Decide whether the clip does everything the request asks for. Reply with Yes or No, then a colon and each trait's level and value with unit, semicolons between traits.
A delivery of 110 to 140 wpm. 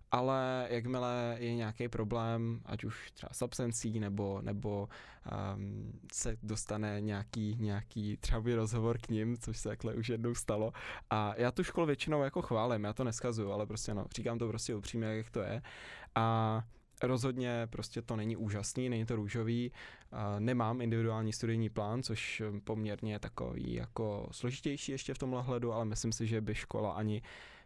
No: fast, 170 wpm